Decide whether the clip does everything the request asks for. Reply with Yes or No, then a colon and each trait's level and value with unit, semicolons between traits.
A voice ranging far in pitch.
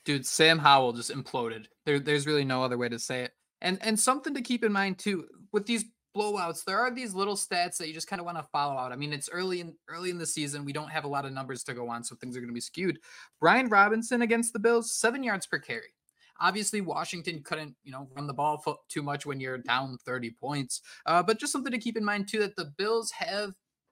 Yes: wide, 6.8 semitones